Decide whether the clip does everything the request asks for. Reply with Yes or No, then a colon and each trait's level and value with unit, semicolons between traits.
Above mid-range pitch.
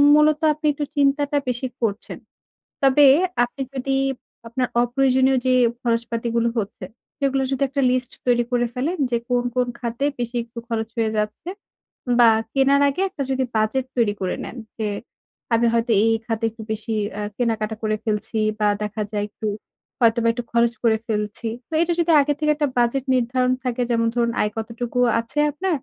Yes: high, 240 Hz